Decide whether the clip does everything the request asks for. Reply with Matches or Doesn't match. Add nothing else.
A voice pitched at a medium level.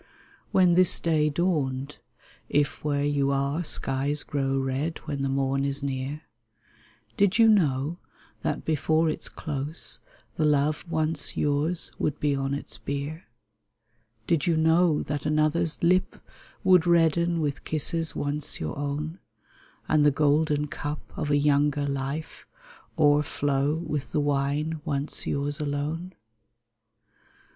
Matches